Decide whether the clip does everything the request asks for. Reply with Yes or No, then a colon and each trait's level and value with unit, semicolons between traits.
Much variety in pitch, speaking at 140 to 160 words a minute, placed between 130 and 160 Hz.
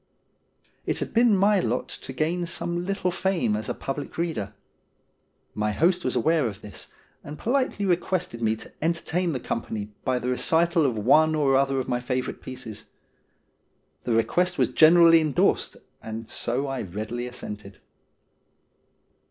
Yes: wide, 6.8 semitones; average, 150 wpm; medium, 140 Hz